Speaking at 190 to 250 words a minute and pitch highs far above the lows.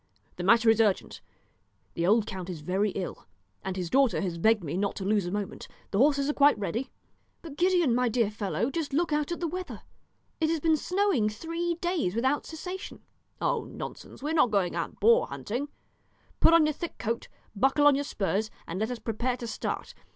Yes: fast, 205 wpm; wide, 7.3 semitones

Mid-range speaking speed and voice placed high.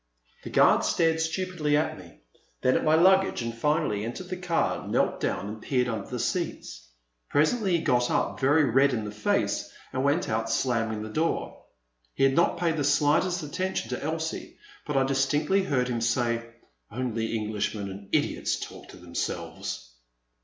No: average, 175 wpm; low, 135 Hz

